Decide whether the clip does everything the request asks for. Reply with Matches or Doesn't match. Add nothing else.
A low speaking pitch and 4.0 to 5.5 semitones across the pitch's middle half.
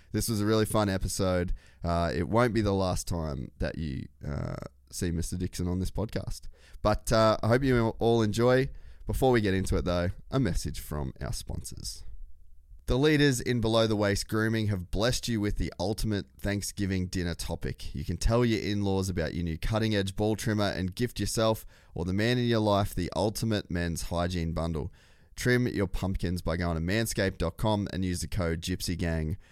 Matches